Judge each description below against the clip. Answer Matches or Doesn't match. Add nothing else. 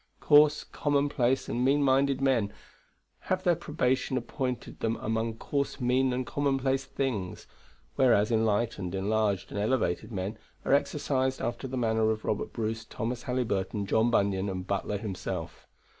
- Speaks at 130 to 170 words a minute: Matches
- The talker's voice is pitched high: Doesn't match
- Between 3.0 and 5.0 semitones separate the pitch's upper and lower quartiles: Matches